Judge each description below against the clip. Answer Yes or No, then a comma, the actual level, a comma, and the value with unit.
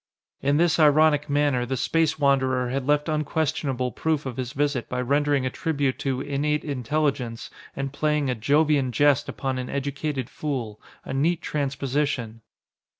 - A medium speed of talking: Yes, average, 150 wpm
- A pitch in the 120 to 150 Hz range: Yes, medium, 140 Hz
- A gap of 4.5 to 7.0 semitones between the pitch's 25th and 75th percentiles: No, narrow, 2.4 semitones